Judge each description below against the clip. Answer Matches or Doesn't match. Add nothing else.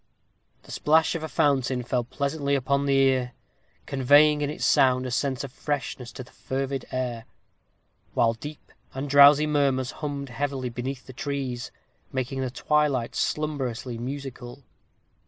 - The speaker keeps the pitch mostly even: Matches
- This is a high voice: Doesn't match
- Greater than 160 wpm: Doesn't match